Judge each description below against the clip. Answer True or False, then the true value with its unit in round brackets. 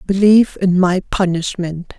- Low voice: False (185 Hz)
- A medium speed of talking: False (120 wpm)